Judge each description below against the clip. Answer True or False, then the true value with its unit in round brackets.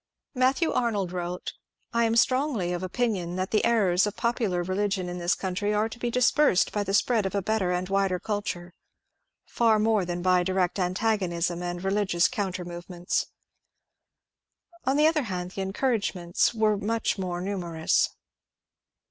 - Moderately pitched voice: False (195 Hz)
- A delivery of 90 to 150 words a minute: False (165 wpm)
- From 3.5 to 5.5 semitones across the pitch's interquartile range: True (3.8 semitones)